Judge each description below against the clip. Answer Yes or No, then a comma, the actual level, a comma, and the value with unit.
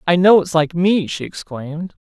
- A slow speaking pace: No, fast, 205 wpm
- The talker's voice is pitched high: No, medium, 170 Hz